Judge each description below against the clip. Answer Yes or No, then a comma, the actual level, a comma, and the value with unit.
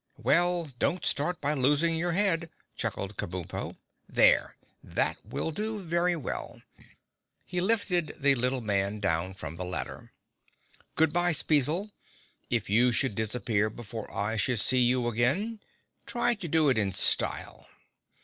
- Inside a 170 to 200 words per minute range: No, average, 140 wpm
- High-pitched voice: No, medium, 140 Hz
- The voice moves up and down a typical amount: No, wide, 8.0 semitones